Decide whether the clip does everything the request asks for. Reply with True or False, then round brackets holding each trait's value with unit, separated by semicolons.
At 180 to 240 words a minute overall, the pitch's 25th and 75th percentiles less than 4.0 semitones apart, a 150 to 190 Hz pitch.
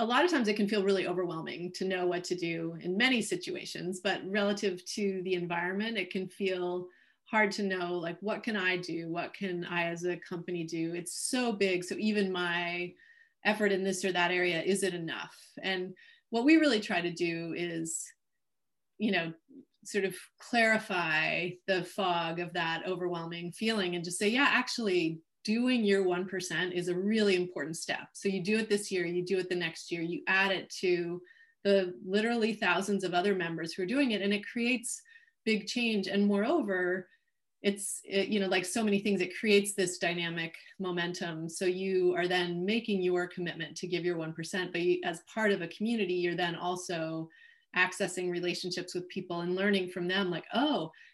True (190 wpm; 2.8 semitones; 185 Hz)